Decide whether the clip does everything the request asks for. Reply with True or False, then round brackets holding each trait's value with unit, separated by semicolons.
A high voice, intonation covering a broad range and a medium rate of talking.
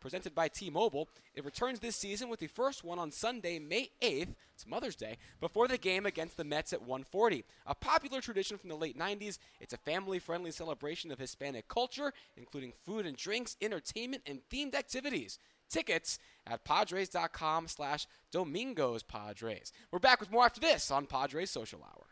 False (180 Hz; 7.6 semitones; 175 wpm)